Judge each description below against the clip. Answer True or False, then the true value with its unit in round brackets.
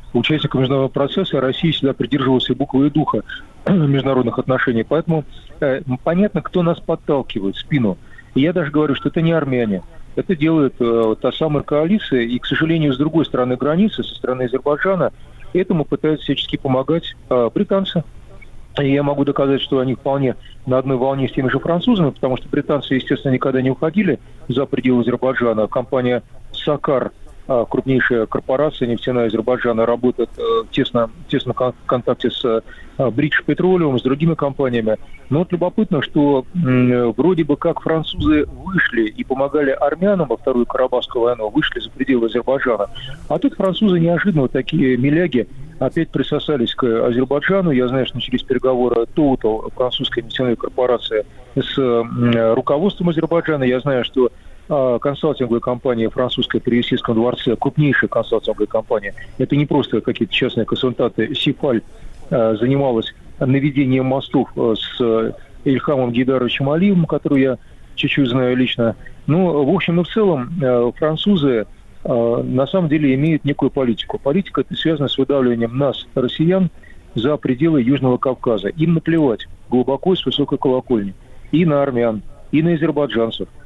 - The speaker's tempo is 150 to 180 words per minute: True (155 wpm)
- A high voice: False (135 Hz)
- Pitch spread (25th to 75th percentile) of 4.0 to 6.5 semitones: False (3.6 semitones)